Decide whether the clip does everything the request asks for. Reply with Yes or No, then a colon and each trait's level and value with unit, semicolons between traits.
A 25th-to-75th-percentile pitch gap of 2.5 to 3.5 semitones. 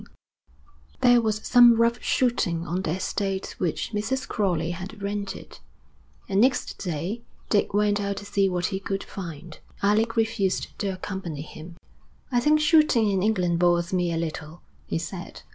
No: average, 4.0 semitones